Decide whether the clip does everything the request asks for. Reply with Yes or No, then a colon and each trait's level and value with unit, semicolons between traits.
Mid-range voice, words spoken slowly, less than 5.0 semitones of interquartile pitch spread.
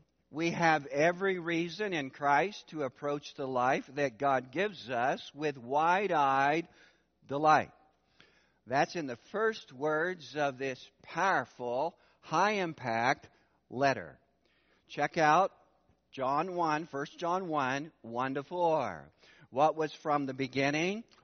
Yes: medium, 150 Hz; slow, 120 wpm; average, 3.7 semitones